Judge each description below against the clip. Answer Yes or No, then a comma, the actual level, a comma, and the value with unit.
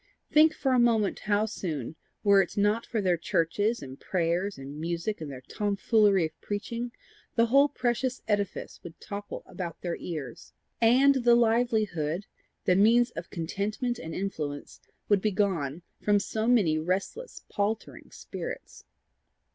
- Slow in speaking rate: No, average, 145 wpm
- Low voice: No, high, 205 Hz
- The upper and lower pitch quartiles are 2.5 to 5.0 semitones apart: No, wide, 5.4 semitones